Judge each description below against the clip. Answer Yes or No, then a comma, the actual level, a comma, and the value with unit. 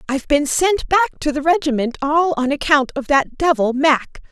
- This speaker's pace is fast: No, average, 195 wpm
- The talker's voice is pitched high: Yes, very high, 295 Hz